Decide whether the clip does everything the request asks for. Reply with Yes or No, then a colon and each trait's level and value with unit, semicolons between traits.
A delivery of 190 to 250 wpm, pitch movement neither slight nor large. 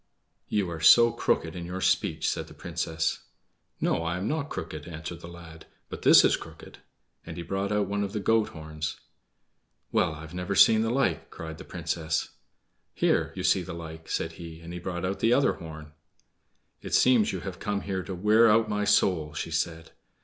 Yes: average, 195 wpm; average, 3.9 semitones